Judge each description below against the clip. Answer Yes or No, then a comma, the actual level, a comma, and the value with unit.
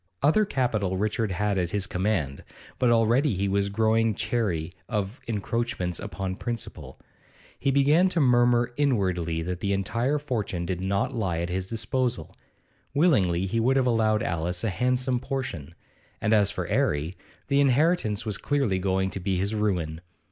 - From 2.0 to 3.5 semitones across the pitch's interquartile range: No, average, 4.8 semitones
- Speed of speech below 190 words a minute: Yes, average, 160 wpm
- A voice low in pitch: Yes, low, 105 Hz